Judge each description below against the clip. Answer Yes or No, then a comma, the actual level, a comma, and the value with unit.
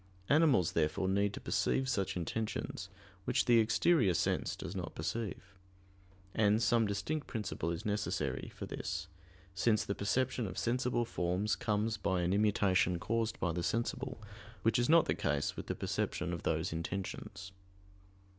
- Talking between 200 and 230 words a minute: No, average, 155 wpm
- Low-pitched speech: Yes, low, 100 Hz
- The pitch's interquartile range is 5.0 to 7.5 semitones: No, average, 4.4 semitones